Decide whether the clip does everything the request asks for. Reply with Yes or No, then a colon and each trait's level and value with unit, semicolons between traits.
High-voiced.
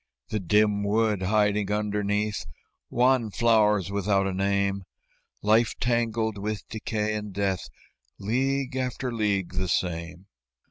No: low, 105 Hz